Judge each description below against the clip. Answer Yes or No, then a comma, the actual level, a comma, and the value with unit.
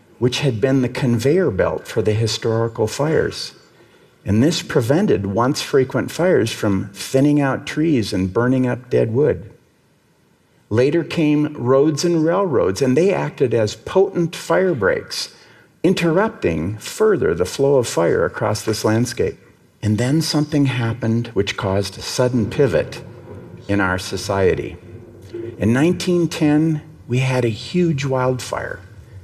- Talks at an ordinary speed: Yes, average, 135 wpm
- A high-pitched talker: No, low, 130 Hz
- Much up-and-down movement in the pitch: Yes, wide, 6.2 semitones